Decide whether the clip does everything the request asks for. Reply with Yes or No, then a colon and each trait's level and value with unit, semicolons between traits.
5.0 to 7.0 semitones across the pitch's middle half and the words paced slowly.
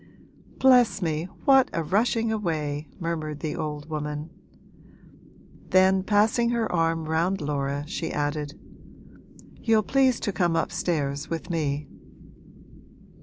Yes: wide, 5.4 semitones; slow, 115 wpm